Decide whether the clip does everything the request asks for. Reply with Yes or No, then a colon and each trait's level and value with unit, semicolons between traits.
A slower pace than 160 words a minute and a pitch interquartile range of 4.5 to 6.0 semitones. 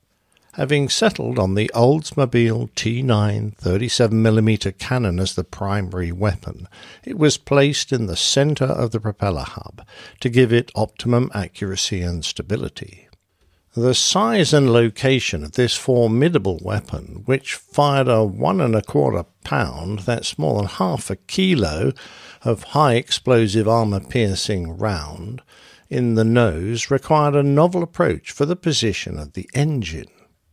Yes: slow, 135 wpm; wide, 5.5 semitones